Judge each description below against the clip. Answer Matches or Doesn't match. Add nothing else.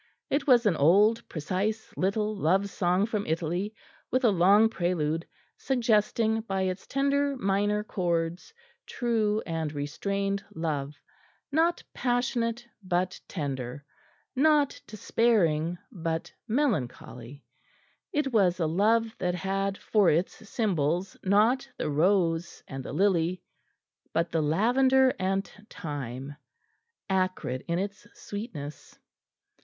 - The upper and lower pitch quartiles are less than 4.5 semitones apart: Doesn't match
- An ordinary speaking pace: Doesn't match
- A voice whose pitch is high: Matches